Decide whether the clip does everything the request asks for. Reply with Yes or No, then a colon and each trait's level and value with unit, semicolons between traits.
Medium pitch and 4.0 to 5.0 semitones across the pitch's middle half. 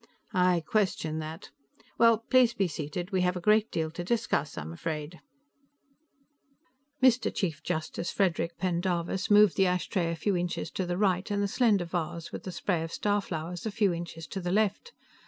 No: medium, 180 Hz; average, 3.3 semitones